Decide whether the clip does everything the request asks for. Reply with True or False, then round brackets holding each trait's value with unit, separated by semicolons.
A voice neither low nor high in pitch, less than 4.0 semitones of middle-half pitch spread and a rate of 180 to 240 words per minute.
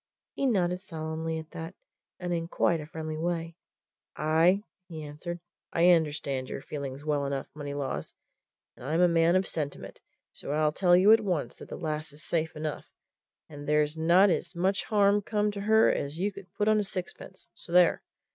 True (165 Hz; 3.4 semitones; 185 wpm)